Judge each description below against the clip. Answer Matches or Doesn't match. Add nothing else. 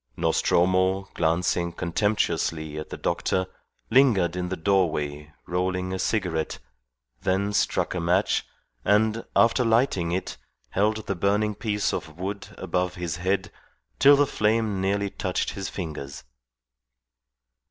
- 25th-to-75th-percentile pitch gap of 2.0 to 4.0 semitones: Matches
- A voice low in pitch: Matches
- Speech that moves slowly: Matches